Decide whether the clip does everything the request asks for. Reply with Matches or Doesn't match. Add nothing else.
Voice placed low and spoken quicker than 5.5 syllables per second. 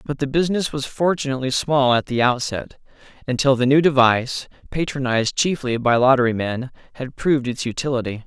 Matches